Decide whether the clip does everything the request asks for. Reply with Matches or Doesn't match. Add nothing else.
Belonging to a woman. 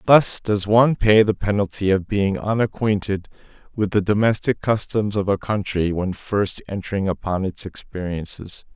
Doesn't match